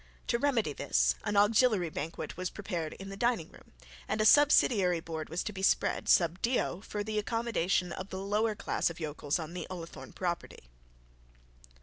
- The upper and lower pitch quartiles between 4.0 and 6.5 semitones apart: Yes, average, 4.4 semitones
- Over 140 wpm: Yes, average, 180 wpm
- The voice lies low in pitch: No, high, 190 Hz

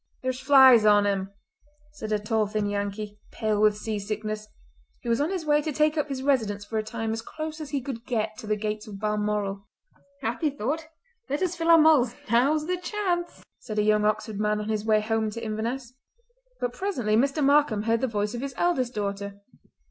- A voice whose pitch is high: Yes, high, 225 Hz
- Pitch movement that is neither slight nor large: Yes, average, 4.9 semitones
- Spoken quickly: Yes, fast, 210 wpm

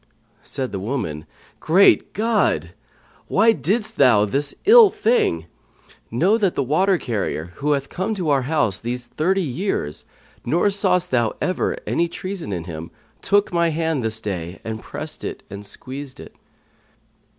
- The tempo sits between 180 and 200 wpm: No, average, 150 wpm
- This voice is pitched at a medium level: Yes, medium, 145 Hz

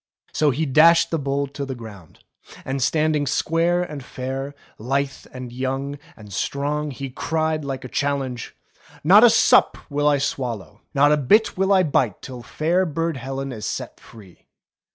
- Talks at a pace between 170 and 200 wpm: Yes, average, 175 wpm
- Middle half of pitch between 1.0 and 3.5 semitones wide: Yes, average, 3.2 semitones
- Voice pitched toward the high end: No, medium, 140 Hz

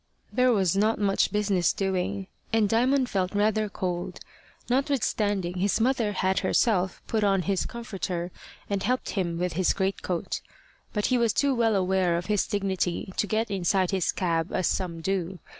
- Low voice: No, high, 195 Hz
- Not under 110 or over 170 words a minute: Yes, average, 165 wpm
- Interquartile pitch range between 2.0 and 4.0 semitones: Yes, average, 2.9 semitones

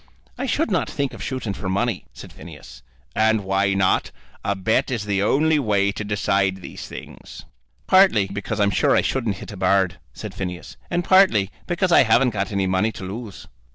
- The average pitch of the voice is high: No, low, 105 Hz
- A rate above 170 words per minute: Yes, average, 190 wpm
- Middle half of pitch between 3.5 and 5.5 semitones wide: Yes, average, 4.3 semitones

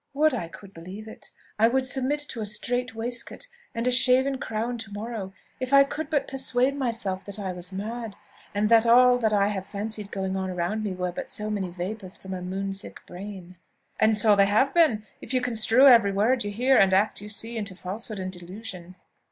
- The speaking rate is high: Yes, fast, 215 wpm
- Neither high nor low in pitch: No, high, 215 Hz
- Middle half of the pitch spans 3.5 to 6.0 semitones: Yes, average, 4.2 semitones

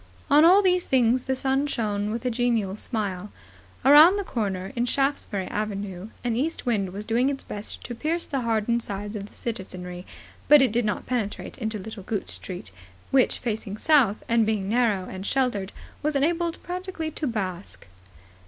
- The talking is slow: No, average, 175 wpm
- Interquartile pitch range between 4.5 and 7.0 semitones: Yes, average, 4.9 semitones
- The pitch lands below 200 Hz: No, high, 230 Hz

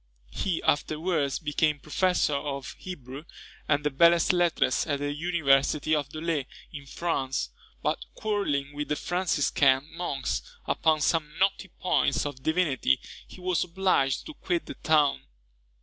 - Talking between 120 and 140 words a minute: Yes, slow, 135 wpm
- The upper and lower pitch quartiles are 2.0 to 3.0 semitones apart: No, average, 3.7 semitones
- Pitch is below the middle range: No, medium, 150 Hz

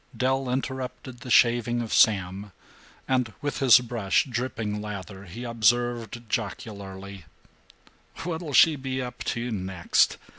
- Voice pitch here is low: Yes, low, 120 Hz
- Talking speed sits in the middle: No, slow, 120 wpm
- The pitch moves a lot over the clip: No, average, 3.9 semitones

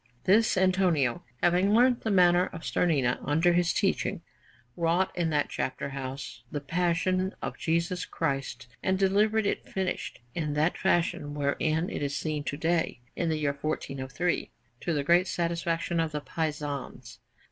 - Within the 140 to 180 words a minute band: Yes, average, 155 wpm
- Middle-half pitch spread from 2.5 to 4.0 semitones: Yes, average, 3.7 semitones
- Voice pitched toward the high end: No, medium, 165 Hz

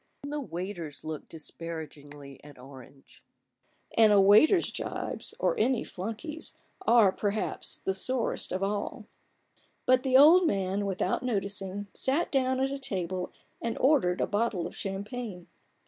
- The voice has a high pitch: Yes, high, 205 Hz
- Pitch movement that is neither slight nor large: No, wide, 6.2 semitones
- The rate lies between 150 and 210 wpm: No, average, 140 wpm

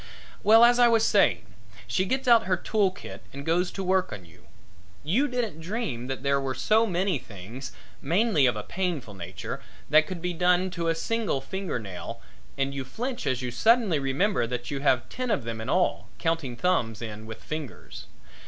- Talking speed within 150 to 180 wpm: No, average, 195 wpm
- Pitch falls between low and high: Yes, medium, 165 Hz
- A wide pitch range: Yes, wide, 7.9 semitones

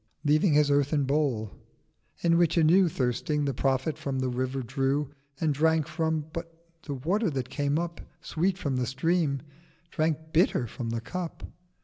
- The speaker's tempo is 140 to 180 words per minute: Yes, average, 165 wpm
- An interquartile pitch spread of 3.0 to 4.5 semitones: Yes, average, 3.4 semitones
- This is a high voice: No, medium, 150 Hz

